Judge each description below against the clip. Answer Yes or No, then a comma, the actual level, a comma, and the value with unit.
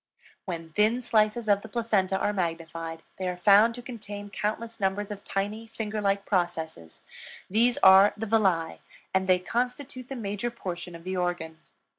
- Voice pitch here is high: Yes, high, 200 Hz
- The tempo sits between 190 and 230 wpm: No, average, 165 wpm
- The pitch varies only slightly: No, average, 3.7 semitones